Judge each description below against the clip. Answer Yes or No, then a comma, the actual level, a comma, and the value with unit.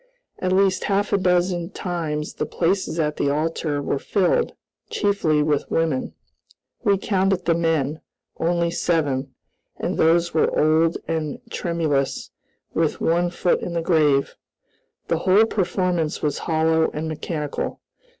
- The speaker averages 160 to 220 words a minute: No, slow, 135 wpm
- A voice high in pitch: No, medium, 165 Hz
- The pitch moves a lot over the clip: No, average, 2.7 semitones